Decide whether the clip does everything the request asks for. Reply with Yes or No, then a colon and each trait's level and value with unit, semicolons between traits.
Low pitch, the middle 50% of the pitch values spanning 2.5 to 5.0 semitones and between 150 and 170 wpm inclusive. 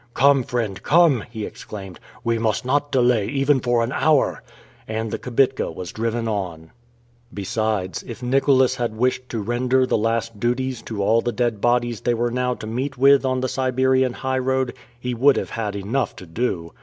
No: low, 120 Hz; average, 2.9 semitones; average, 180 wpm